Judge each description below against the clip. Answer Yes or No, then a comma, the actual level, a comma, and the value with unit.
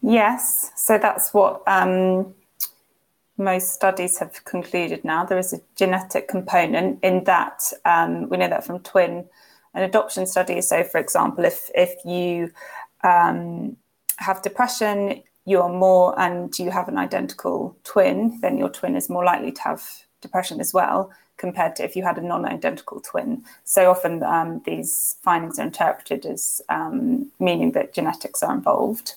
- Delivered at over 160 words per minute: No, average, 155 wpm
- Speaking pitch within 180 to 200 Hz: Yes, high, 190 Hz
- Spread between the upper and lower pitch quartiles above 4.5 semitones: No, average, 3.4 semitones